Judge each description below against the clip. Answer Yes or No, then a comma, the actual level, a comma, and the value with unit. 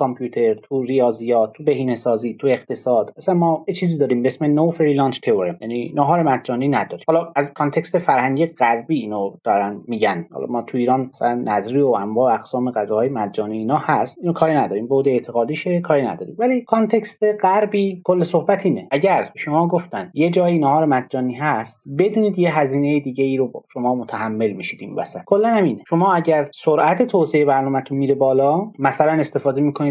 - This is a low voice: No, medium, 145 Hz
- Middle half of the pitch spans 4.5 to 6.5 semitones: Yes, average, 5.1 semitones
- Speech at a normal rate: No, fast, 175 wpm